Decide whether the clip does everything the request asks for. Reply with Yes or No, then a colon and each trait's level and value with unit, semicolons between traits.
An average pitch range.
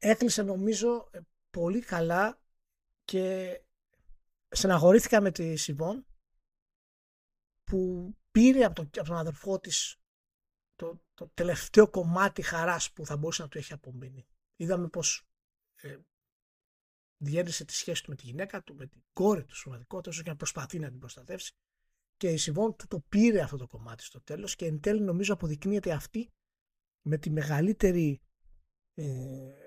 Yes: average, 5.0 semitones